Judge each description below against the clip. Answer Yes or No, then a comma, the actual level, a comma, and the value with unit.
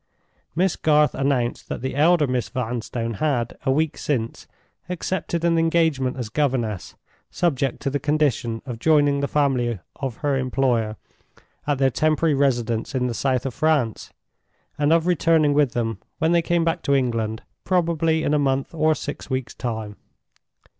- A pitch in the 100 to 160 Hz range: Yes, medium, 140 Hz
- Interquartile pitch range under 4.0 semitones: No, average, 4.3 semitones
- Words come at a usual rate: Yes, average, 160 wpm